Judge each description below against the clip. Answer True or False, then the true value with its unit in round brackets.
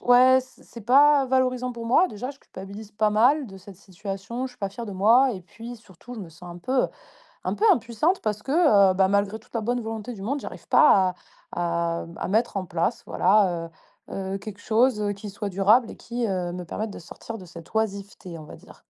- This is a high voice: True (215 Hz)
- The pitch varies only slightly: False (4.1 semitones)